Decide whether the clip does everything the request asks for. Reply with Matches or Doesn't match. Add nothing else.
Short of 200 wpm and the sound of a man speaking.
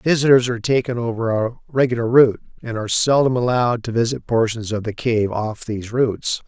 Matches